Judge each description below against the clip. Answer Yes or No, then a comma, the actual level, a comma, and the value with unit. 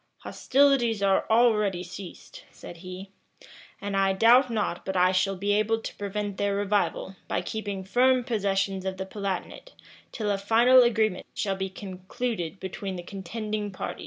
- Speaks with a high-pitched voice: Yes, high, 200 Hz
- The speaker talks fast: No, average, 160 wpm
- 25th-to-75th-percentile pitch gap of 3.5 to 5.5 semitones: No, average, 2.7 semitones